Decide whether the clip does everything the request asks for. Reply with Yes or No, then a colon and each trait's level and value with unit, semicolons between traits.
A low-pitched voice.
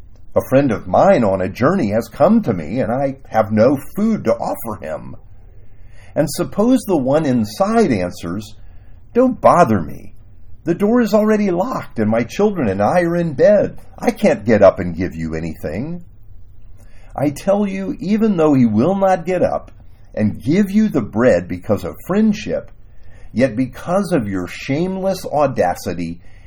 Yes: low, 120 Hz